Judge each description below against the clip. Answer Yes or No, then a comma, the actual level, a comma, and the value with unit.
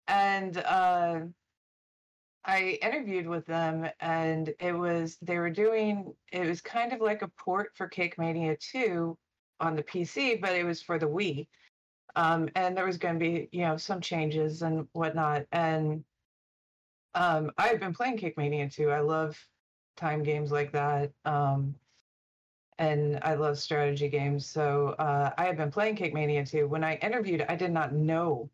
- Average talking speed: Yes, average, 170 wpm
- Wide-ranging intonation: No, average, 2.9 semitones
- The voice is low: No, medium, 165 Hz